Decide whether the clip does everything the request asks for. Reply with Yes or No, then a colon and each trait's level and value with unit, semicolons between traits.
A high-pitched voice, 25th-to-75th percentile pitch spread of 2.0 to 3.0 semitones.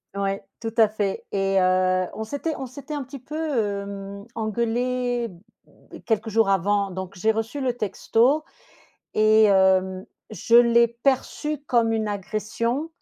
No: high, 220 Hz; average, 3.6 semitones